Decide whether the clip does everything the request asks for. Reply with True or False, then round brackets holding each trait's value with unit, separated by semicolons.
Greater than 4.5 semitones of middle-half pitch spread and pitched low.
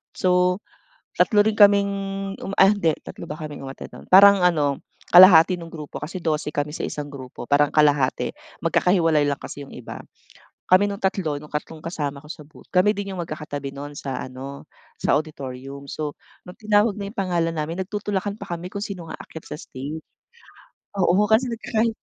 False (5.2 semitones; 165 Hz)